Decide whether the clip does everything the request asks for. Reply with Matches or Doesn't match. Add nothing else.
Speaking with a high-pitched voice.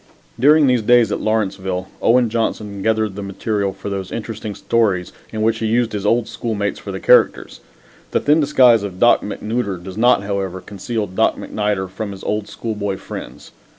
Doesn't match